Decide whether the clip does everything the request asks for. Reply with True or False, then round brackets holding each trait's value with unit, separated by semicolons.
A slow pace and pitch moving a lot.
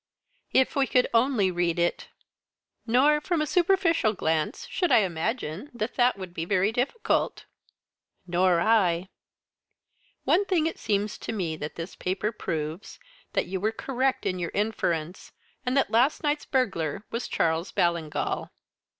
False (150 wpm; 7.1 semitones)